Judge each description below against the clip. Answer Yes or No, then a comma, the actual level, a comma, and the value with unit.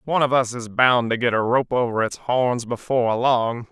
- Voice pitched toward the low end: Yes, low, 120 Hz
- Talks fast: Yes, fast, 225 wpm